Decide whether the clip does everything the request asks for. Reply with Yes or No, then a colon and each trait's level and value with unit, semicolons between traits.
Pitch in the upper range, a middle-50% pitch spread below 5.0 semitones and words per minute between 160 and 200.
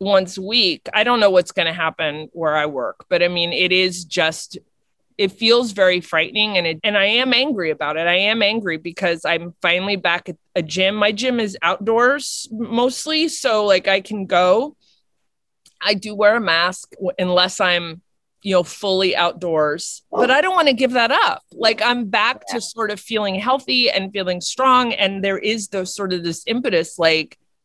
Yes: high, 195 Hz; average, 4.4 semitones; average, 190 wpm